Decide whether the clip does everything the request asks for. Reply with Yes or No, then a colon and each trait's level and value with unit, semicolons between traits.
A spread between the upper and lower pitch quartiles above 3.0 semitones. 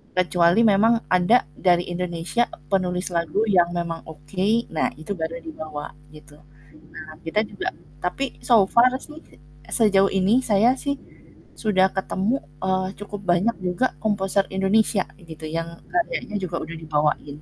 Yes: average, 3.8 semitones